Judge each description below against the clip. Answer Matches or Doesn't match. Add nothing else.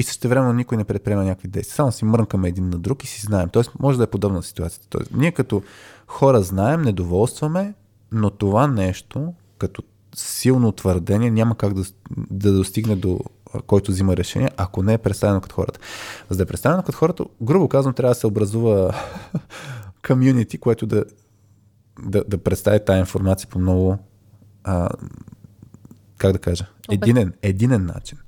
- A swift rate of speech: Matches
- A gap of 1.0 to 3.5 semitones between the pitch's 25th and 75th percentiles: Doesn't match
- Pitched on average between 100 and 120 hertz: Matches